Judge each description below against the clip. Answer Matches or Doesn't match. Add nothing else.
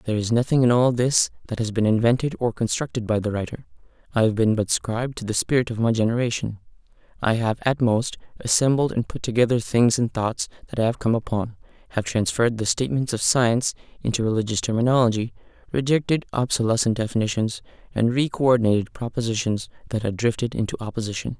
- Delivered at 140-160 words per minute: Doesn't match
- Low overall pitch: Matches